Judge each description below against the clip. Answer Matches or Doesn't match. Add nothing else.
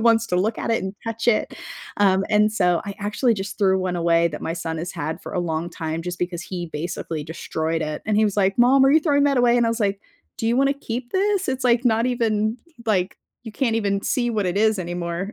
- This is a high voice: Matches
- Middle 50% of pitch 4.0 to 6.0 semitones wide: Matches